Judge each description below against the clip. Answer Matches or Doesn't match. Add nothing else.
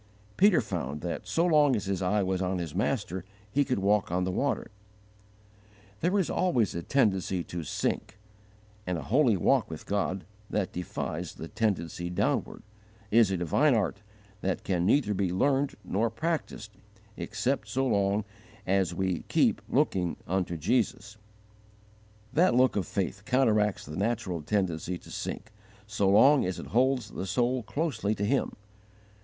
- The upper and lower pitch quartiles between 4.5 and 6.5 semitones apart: Matches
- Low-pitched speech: Matches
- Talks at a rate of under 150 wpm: Doesn't match